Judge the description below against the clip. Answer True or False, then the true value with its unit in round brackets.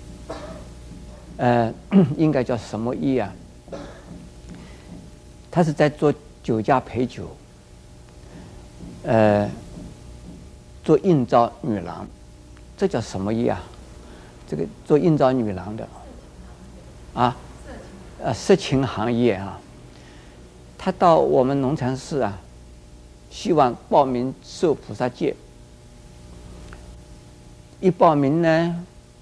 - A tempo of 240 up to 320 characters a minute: False (130 characters per minute)